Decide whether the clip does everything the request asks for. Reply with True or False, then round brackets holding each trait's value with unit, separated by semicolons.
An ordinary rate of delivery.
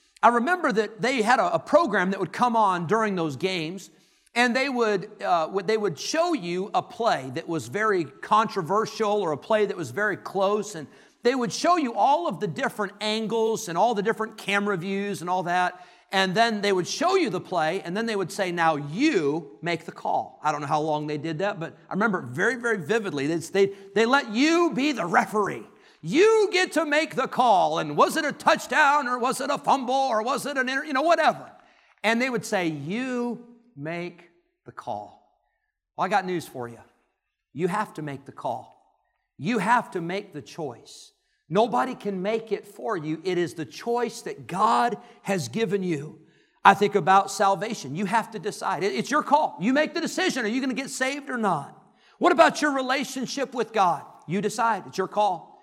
False (210 wpm)